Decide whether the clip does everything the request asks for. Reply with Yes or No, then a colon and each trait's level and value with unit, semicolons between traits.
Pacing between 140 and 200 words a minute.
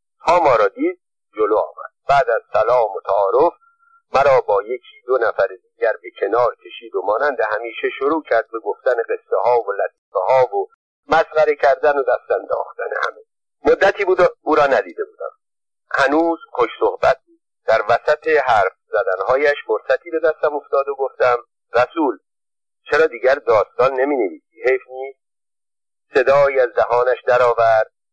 Yes: fast, 155 wpm